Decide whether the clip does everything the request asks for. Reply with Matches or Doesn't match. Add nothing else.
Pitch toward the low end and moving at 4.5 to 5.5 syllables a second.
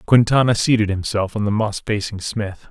Matches